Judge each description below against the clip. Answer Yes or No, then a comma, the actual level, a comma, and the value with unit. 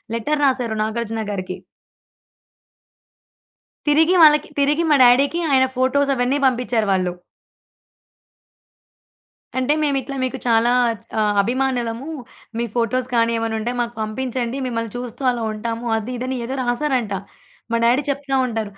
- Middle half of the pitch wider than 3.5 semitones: No, average, 2.9 semitones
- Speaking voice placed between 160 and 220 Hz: No, high, 245 Hz